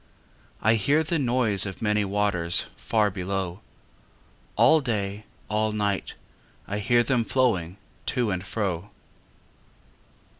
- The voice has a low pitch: Yes, low, 105 Hz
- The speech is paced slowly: Yes, slow, 115 wpm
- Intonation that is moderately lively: Yes, average, 3.4 semitones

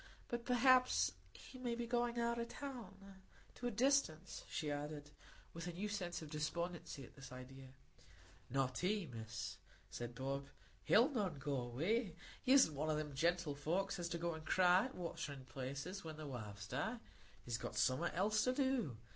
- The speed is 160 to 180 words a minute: Yes, average, 170 wpm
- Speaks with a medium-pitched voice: Yes, medium, 170 Hz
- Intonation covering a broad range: Yes, wide, 7.9 semitones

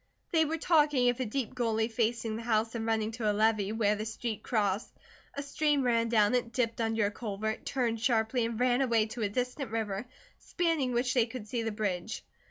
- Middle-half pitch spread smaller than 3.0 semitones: Yes, narrow, 2.4 semitones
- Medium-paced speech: No, fast, 210 wpm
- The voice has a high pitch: Yes, high, 230 Hz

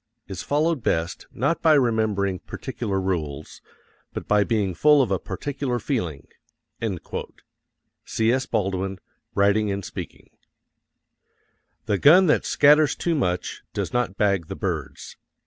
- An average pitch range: No, wide, 6.5 semitones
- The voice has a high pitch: No, low, 105 Hz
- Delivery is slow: Yes, slow, 125 wpm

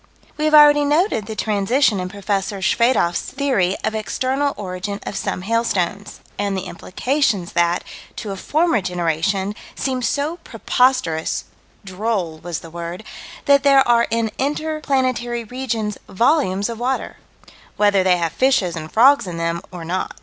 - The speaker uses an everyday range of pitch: No, wide, 6.2 semitones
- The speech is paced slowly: No, average, 150 wpm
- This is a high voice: Yes, high, 210 Hz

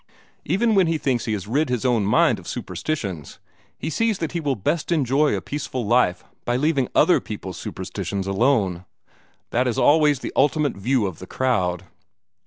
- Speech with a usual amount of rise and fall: No, wide, 6.6 semitones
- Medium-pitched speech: No, low, 130 Hz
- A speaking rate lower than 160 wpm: No, average, 180 wpm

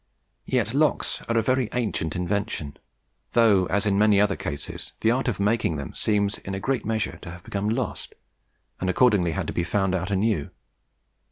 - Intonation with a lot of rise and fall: No, average, 3.2 semitones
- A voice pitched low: Yes, low, 100 Hz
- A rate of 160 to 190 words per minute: Yes, average, 185 wpm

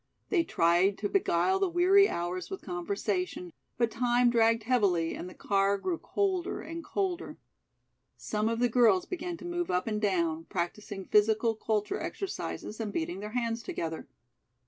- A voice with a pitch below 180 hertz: No, high, 220 Hz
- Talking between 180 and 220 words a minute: No, average, 160 wpm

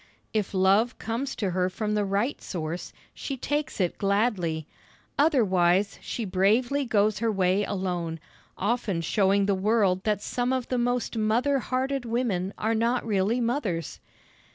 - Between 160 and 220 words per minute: No, average, 150 wpm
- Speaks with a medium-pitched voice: No, high, 210 Hz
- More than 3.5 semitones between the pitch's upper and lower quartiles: Yes, average, 4.3 semitones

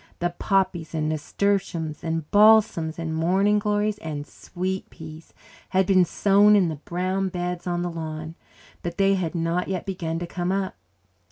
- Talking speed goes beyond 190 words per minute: No, average, 165 wpm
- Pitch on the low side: No, medium, 175 Hz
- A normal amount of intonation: Yes, average, 3.0 semitones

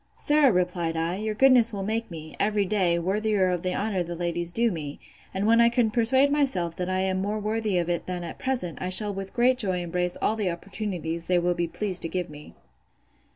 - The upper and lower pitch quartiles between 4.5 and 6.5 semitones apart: No, average, 3.9 semitones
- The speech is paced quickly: Yes, fast, 225 wpm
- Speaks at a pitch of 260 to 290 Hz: No, high, 190 Hz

